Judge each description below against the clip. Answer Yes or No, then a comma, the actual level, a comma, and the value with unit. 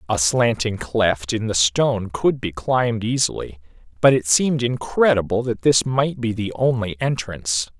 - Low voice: Yes, low, 110 Hz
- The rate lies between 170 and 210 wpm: No, average, 160 wpm